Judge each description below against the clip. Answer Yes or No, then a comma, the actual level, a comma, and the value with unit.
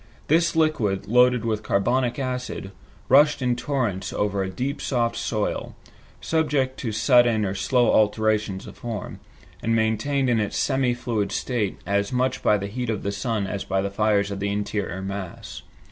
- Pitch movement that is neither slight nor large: Yes, average, 3.9 semitones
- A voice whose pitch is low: Yes, low, 110 Hz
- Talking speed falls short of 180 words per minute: Yes, average, 170 wpm